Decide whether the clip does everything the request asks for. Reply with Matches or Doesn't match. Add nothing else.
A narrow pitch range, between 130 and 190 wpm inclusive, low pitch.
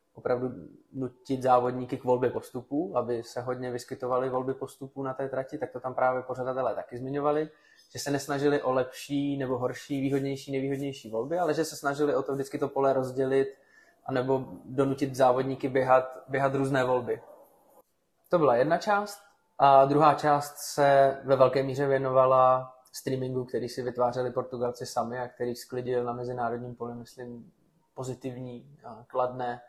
Matches